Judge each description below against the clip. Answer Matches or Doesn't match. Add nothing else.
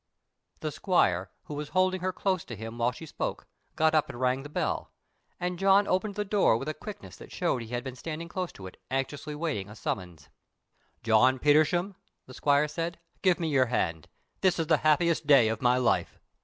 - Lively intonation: Matches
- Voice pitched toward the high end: Doesn't match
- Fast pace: Matches